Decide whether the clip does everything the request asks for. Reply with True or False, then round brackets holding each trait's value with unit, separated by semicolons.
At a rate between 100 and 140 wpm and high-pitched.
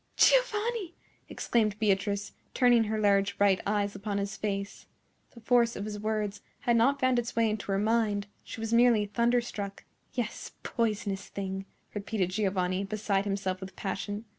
False (155 wpm; 210 Hz)